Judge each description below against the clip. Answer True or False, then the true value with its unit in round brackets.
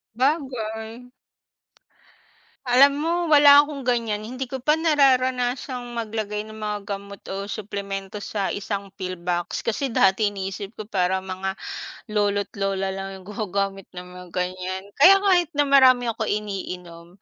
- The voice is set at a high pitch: True (210 Hz)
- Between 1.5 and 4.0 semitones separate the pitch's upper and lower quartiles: False (4.7 semitones)